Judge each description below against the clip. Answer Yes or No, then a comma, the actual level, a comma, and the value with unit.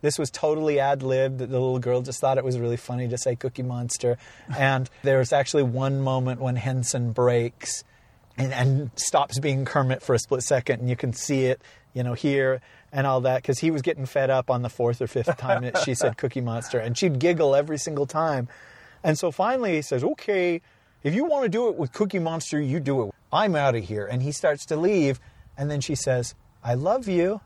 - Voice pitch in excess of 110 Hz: Yes, low, 135 Hz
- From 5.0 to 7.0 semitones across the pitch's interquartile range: No, average, 3.1 semitones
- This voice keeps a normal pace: No, fast, 225 wpm